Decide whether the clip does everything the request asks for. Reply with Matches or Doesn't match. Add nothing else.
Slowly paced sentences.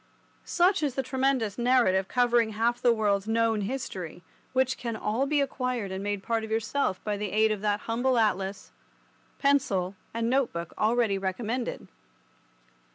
Doesn't match